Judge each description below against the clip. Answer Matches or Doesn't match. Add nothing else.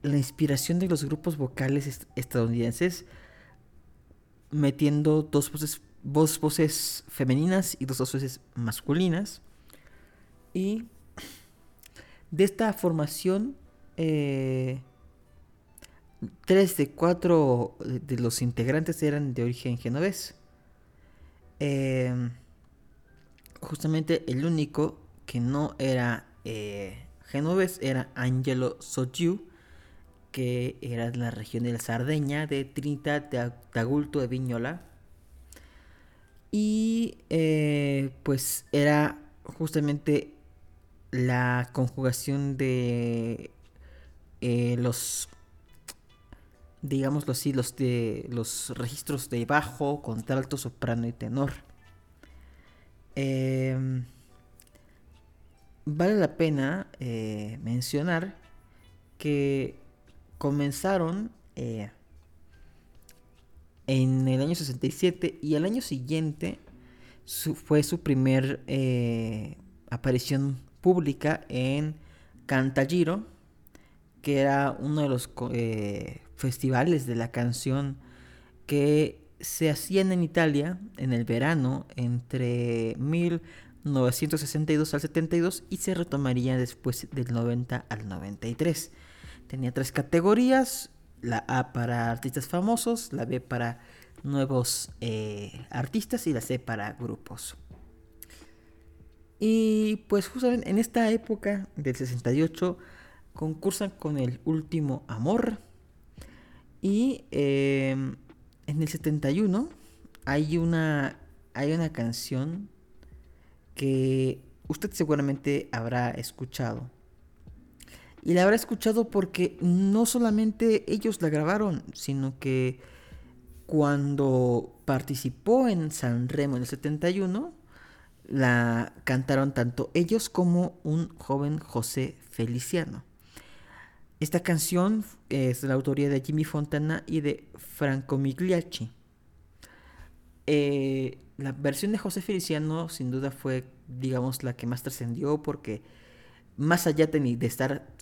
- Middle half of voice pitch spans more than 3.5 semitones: Matches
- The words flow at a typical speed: Doesn't match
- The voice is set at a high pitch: Doesn't match